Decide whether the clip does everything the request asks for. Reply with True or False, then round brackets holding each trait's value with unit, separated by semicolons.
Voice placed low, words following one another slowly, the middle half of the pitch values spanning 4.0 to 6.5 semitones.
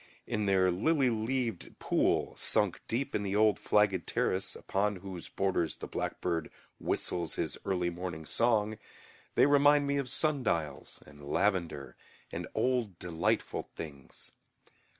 True (100 Hz; 130 wpm; 5.6 semitones)